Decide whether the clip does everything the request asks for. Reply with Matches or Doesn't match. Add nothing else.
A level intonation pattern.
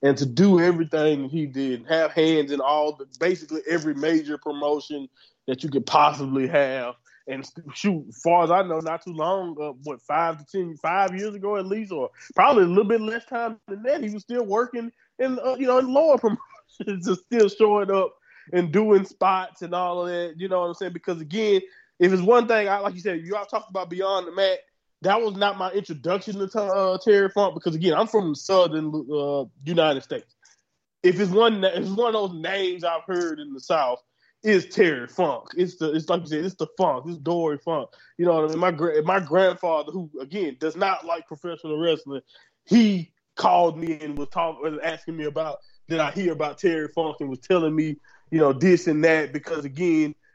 Doesn't match